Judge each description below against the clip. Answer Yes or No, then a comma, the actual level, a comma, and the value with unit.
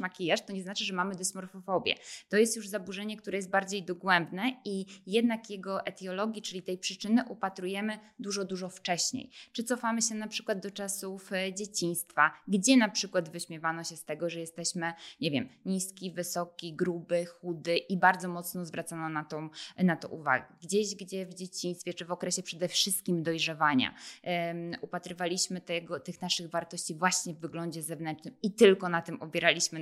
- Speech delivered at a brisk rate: Yes, fast, 165 wpm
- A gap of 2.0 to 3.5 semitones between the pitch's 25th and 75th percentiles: Yes, narrow, 2.6 semitones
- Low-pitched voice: No, medium, 185 Hz